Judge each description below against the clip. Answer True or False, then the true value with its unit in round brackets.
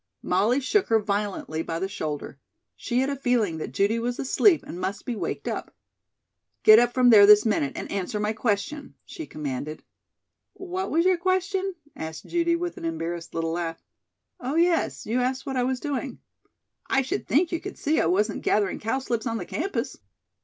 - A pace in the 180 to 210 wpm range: True (190 wpm)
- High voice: True (235 Hz)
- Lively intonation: True (7.3 semitones)